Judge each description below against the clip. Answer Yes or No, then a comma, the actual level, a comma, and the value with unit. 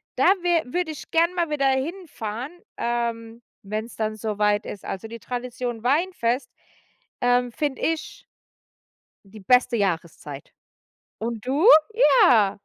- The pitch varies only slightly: No, average, 4.8 semitones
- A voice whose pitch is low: No, high, 240 Hz